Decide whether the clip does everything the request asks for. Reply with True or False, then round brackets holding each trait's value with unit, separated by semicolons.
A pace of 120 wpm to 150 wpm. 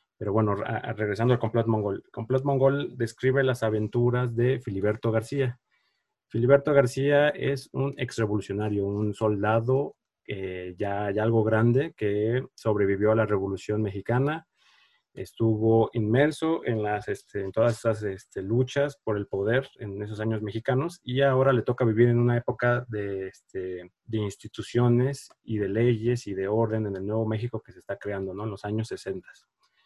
False (160 wpm)